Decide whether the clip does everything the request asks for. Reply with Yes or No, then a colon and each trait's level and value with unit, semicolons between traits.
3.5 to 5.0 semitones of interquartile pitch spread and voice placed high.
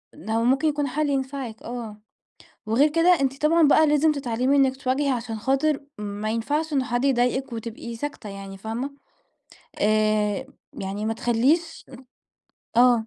Yes: average, 4.2 semitones; very high, 250 Hz